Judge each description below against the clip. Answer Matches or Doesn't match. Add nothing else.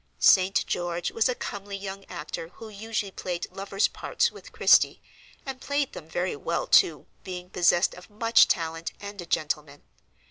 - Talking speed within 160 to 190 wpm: Matches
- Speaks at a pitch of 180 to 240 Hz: Matches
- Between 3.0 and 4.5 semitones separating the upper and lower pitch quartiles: Matches